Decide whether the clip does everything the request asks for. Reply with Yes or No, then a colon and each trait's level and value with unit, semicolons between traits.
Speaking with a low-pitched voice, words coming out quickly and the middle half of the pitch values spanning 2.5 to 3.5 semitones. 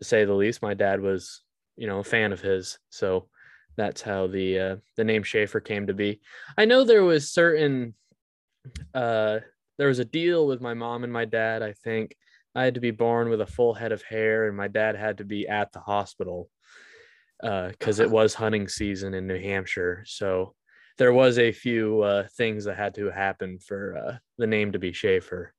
Yes: low, 110 Hz; fast, 210 wpm; average, 3.0 semitones